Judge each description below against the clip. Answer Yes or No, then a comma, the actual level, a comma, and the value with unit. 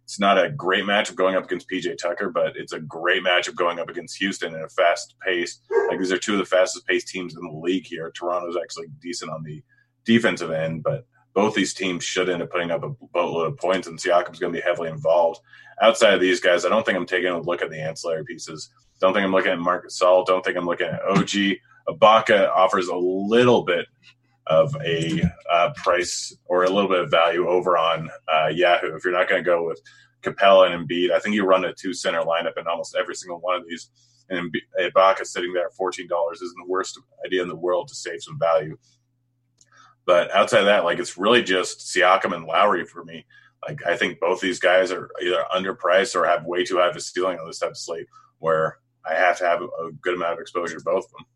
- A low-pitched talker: Yes, very low, 95 Hz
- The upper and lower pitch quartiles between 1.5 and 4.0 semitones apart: No, average, 5.1 semitones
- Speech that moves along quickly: Yes, fast, 235 wpm